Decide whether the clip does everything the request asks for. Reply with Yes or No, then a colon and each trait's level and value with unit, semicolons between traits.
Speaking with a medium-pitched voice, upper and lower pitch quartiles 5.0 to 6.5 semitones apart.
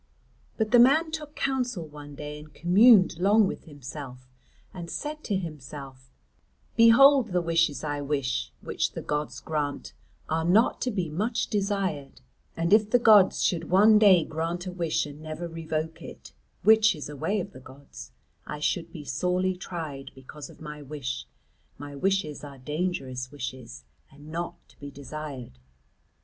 Yes: medium, 160 Hz; average, 5.3 semitones